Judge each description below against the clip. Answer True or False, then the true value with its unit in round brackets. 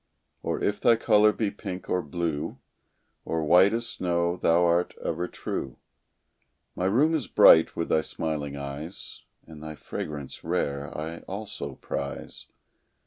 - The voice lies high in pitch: False (85 Hz)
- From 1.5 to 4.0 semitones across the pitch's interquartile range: False (4.4 semitones)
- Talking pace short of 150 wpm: True (140 wpm)